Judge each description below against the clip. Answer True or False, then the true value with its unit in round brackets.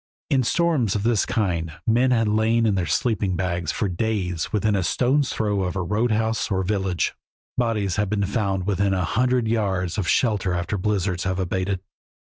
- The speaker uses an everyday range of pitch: True (3.3 semitones)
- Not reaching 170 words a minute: False (185 wpm)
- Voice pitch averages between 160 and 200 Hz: False (100 Hz)